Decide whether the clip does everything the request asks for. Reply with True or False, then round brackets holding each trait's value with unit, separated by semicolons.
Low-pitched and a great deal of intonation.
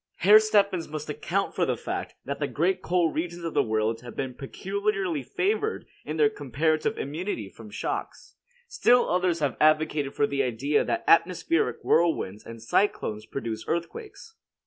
False (160 Hz; 5.9 semitones)